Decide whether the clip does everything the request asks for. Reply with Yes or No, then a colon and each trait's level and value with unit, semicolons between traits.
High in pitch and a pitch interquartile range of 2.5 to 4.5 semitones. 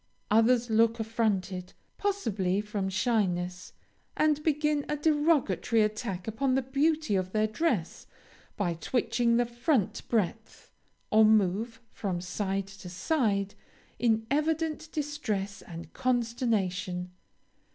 No: high, 225 Hz; average, 5.3 semitones